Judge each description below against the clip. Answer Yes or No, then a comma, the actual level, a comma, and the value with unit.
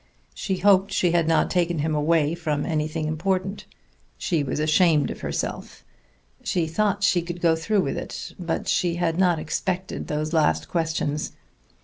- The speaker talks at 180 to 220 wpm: No, average, 160 wpm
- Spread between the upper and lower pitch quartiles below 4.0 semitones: Yes, average, 2.7 semitones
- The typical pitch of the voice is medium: Yes, medium, 165 Hz